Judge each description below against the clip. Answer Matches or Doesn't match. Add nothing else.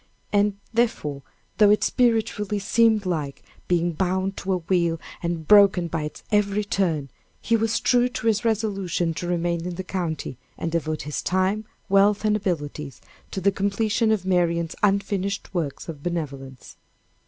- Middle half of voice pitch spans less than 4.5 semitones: Matches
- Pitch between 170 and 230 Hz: Matches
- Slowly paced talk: Doesn't match